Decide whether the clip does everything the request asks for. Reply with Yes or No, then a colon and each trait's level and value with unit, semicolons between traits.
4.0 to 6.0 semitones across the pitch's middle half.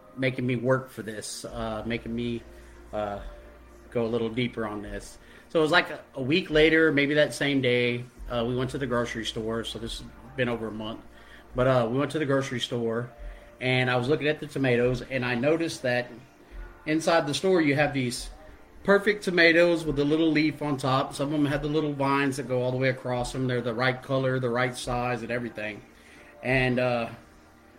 No: average, 3.4 semitones